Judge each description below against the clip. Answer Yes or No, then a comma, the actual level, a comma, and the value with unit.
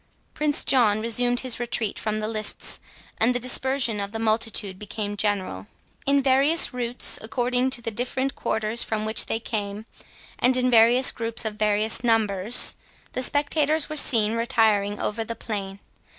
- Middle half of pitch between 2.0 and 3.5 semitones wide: Yes, average, 2.8 semitones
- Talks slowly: No, average, 155 wpm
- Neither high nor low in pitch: No, high, 230 Hz